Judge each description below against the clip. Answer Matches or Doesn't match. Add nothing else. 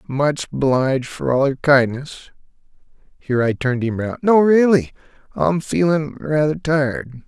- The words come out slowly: Matches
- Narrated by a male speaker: Matches